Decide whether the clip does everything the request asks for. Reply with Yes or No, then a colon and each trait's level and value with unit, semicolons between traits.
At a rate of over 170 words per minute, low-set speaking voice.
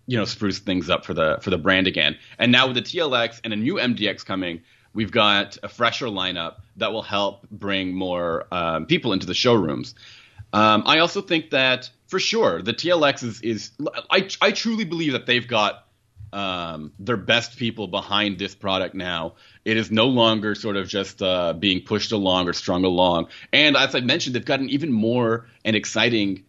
Yes: average, 195 wpm; low, 105 Hz